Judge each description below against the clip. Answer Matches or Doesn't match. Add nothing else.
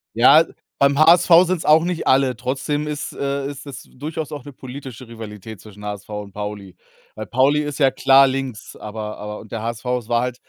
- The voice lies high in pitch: Doesn't match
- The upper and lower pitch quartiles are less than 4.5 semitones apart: Doesn't match